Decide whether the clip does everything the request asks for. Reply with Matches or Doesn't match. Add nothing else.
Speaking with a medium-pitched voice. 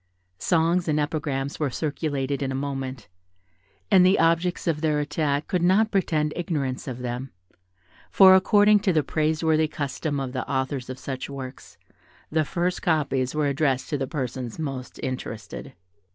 Matches